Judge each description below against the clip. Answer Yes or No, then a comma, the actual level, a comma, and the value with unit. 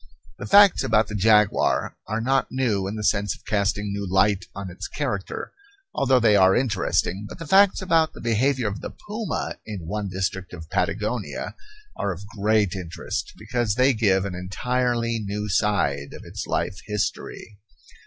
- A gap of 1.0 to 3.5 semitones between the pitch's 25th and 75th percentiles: No, average, 4.0 semitones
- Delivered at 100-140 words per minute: No, average, 170 wpm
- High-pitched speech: No, low, 105 Hz